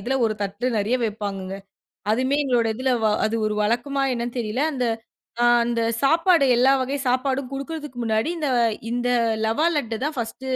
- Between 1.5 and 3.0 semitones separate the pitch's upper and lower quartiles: No, average, 3.6 semitones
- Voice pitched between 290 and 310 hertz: No, high, 245 Hz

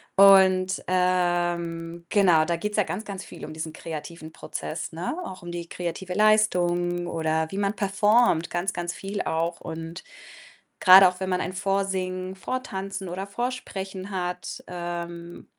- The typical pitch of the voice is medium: Yes, medium, 180 Hz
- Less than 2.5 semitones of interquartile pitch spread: Yes, narrow, 2.1 semitones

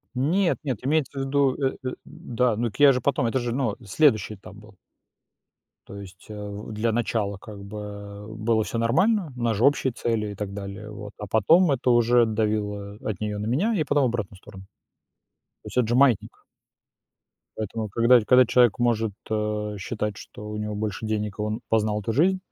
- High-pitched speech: No, low, 110 Hz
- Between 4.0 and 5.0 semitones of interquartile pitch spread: No, average, 3.3 semitones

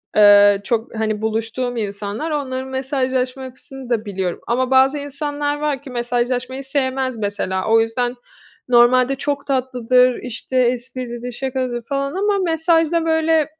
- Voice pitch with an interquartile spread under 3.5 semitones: Yes, average, 2.7 semitones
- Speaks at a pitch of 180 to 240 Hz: No, very high, 255 Hz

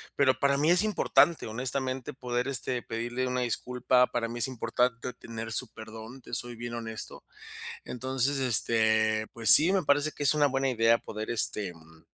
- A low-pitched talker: Yes, low, 125 Hz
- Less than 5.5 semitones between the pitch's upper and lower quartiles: Yes, average, 2.7 semitones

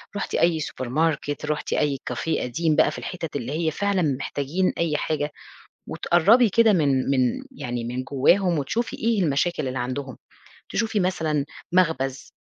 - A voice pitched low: No, medium, 155 Hz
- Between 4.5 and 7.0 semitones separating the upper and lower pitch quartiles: Yes, average, 5.0 semitones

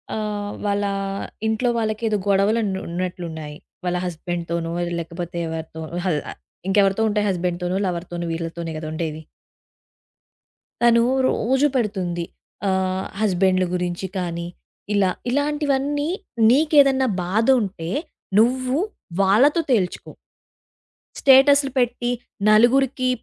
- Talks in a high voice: Yes, high, 195 Hz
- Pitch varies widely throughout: Yes, wide, 5.9 semitones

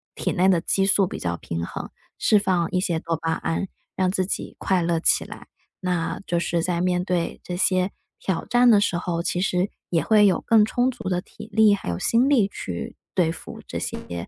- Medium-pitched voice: Yes, medium, 180 Hz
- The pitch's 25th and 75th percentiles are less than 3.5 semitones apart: Yes, average, 3.0 semitones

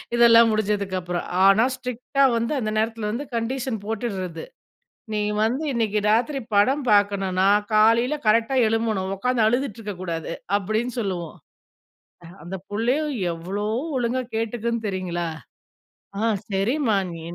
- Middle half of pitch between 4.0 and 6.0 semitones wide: No, average, 3.3 semitones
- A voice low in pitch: No, high, 220 Hz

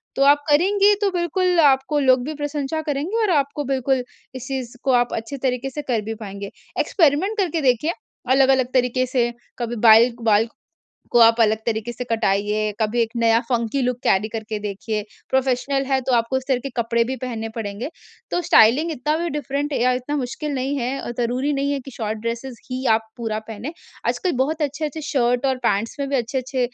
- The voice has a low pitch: No, very high, 255 Hz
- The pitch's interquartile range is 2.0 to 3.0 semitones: No, average, 3.7 semitones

